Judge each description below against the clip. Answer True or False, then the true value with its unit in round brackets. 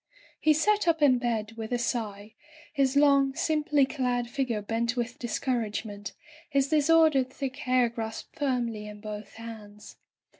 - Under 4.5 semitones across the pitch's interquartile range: True (4.0 semitones)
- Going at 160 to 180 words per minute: False (150 wpm)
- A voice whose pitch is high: True (245 Hz)